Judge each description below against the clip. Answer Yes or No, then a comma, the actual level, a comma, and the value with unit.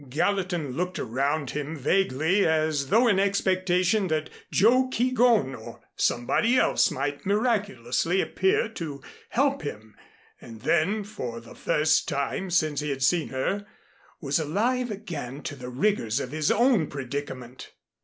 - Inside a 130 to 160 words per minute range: Yes, average, 140 wpm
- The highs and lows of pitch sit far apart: Yes, wide, 6.7 semitones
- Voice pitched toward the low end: No, medium, 160 Hz